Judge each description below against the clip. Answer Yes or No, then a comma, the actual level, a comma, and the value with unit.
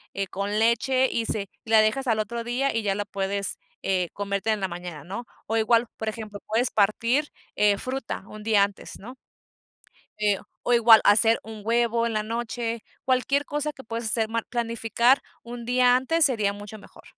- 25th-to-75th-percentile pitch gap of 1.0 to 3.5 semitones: Yes, average, 2.8 semitones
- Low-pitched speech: No, high, 225 Hz